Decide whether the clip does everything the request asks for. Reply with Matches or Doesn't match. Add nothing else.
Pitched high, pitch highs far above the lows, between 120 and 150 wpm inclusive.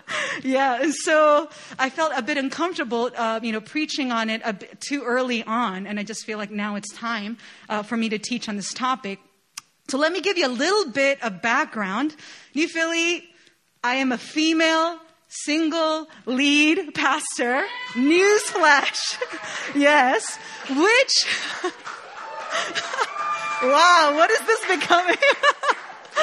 Matches